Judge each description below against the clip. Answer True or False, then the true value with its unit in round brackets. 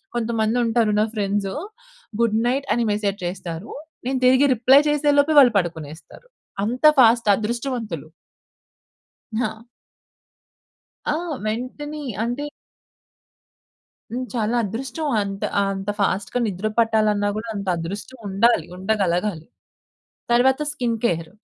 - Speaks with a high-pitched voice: True (225 Hz)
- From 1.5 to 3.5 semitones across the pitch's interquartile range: False (4.0 semitones)